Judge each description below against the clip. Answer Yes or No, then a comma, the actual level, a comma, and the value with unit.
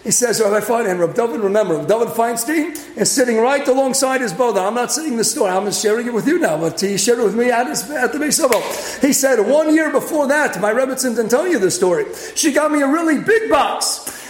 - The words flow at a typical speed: No, fast, 245 wpm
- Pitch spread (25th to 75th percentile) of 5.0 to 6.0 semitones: Yes, wide, 5.5 semitones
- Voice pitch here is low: No, very high, 255 Hz